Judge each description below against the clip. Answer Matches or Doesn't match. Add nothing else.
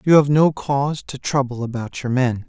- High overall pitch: Doesn't match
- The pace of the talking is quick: Matches